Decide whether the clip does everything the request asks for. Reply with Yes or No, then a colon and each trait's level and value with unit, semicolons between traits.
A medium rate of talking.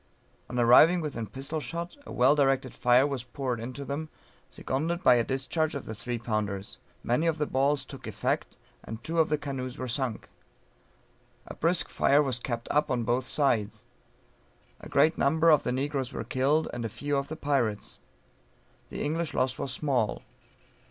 Yes: average, 180 wpm